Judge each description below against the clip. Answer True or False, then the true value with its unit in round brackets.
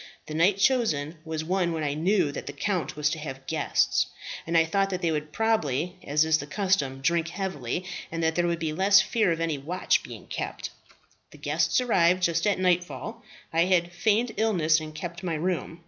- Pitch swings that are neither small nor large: True (3.5 semitones)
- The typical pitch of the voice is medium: True (170 Hz)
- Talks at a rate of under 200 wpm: False (205 wpm)